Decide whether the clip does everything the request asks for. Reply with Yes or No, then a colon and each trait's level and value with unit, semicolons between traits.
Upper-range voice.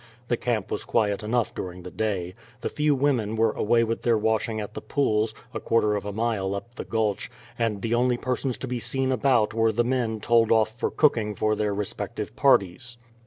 No: low, 115 Hz